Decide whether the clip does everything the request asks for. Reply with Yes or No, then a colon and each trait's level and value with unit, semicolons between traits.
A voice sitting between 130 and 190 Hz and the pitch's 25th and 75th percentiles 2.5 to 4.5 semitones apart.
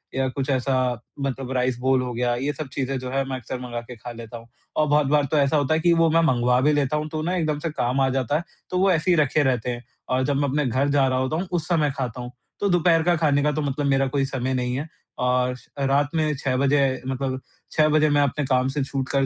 Yes: low, 135 Hz; average, 2.8 semitones